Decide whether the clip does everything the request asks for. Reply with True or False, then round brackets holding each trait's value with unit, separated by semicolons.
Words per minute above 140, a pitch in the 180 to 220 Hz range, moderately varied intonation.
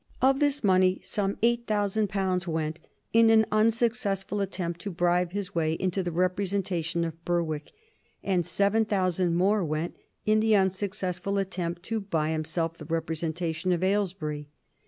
True (150 wpm; 185 Hz; 3.3 semitones)